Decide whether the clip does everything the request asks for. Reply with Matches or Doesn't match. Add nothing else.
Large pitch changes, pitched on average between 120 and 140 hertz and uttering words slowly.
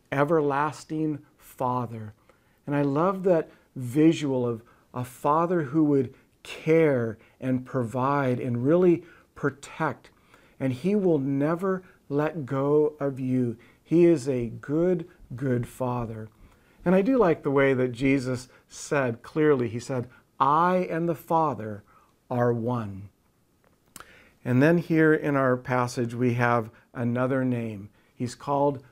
Doesn't match